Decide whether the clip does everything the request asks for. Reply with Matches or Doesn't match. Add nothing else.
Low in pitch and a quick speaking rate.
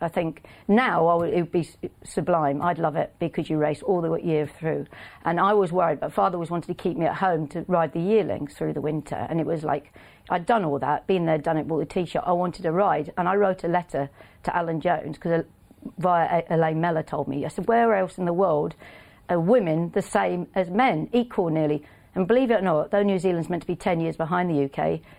Doesn't match